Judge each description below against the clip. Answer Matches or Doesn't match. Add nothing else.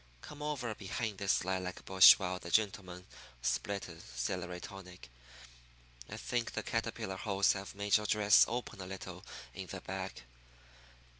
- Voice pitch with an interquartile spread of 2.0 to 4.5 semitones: Matches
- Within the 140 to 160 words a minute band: Matches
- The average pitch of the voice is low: Matches